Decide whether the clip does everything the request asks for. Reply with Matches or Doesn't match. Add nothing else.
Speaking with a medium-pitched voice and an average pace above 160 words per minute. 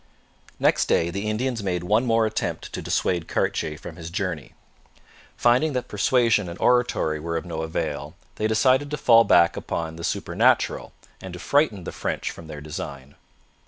Doesn't match